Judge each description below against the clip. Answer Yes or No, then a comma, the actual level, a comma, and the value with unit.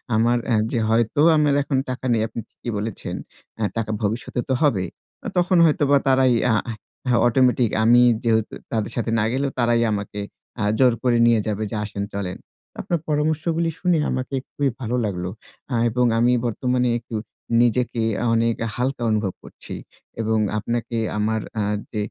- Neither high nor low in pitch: No, low, 120 Hz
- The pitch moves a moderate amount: Yes, average, 3.0 semitones